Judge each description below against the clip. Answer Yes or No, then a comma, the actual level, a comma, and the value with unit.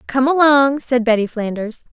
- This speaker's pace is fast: No, average, 150 wpm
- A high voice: Yes, very high, 255 Hz